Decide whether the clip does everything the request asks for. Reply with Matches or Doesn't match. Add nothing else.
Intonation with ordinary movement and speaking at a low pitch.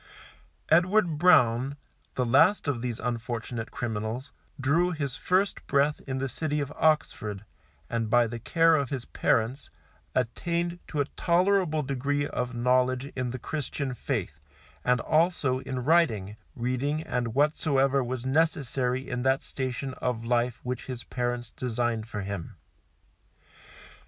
Matches